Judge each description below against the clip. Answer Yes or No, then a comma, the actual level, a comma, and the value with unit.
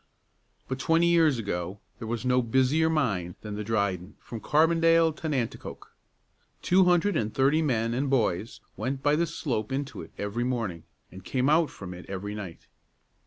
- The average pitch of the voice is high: No, low, 125 Hz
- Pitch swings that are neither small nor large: No, wide, 6.8 semitones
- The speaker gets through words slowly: No, average, 170 wpm